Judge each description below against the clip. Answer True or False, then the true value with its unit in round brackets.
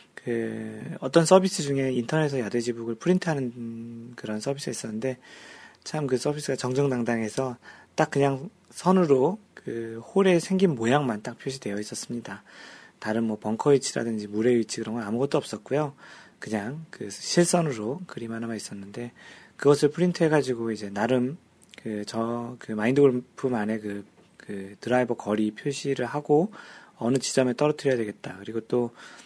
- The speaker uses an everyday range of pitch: True (4.5 semitones)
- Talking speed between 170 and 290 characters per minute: False (340 characters per minute)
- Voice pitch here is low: True (125 Hz)